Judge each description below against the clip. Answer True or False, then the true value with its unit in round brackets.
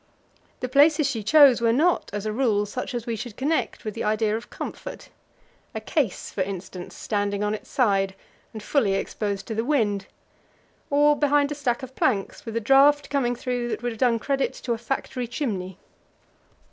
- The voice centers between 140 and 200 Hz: False (235 Hz)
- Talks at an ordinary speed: True (190 wpm)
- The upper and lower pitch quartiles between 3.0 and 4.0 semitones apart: False (4.7 semitones)